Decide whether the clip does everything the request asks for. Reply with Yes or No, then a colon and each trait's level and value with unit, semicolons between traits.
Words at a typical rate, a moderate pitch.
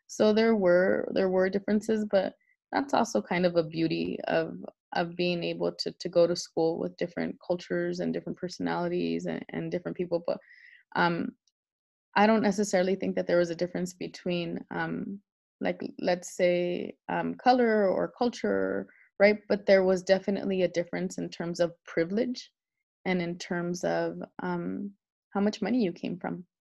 Yes: average, 165 wpm; medium, 180 Hz